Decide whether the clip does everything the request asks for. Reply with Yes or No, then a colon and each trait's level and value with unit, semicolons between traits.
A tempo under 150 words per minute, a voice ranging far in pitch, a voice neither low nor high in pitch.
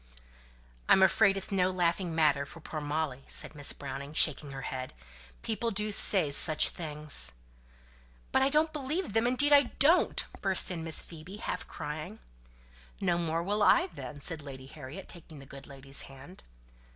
No: average, 165 wpm; wide, 5.8 semitones; medium, 165 Hz